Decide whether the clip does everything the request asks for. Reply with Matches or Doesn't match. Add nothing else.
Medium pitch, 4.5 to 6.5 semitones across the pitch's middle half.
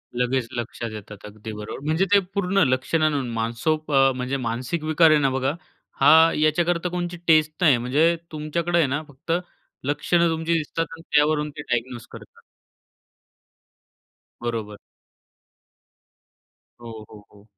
Matches